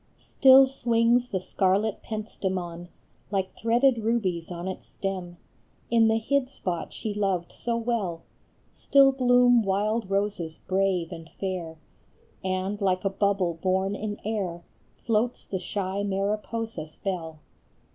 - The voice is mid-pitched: No, high, 200 Hz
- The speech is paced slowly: Yes, slow, 130 wpm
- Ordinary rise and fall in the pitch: Yes, average, 3.6 semitones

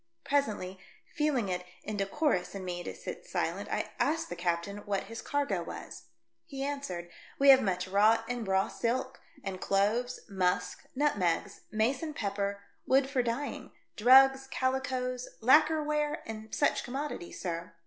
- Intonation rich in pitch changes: Yes, wide, 5.8 semitones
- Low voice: No, high, 230 Hz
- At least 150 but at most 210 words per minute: Yes, average, 155 wpm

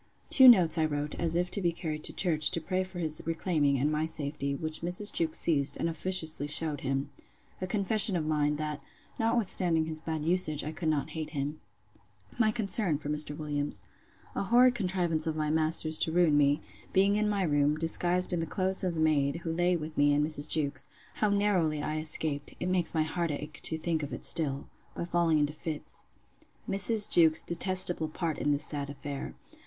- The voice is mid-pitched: Yes, medium, 160 Hz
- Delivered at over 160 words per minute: Yes, average, 200 wpm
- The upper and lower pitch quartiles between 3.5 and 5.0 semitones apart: No, average, 3.0 semitones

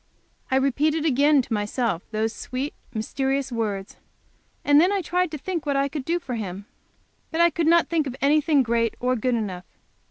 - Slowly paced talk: No, average, 190 wpm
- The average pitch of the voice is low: No, very high, 270 Hz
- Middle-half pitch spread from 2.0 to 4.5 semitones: No, average, 5.0 semitones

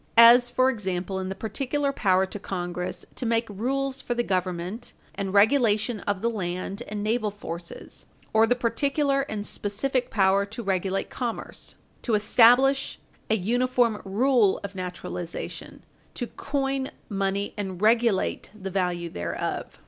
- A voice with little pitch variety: No, average, 4.2 semitones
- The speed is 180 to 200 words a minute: No, average, 140 wpm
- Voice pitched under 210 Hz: No, high, 215 Hz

